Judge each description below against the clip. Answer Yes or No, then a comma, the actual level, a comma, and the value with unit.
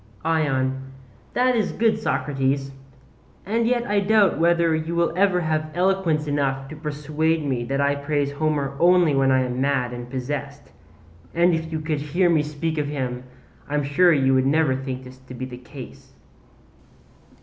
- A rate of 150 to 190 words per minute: Yes, average, 175 wpm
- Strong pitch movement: No, average, 3.8 semitones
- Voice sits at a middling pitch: Yes, medium, 150 Hz